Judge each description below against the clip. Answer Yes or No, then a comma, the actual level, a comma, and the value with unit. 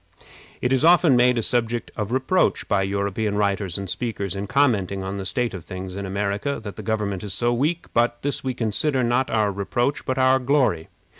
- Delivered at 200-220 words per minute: Yes, fast, 205 wpm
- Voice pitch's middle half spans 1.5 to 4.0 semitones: No, average, 4.4 semitones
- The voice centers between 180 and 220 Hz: No, low, 110 Hz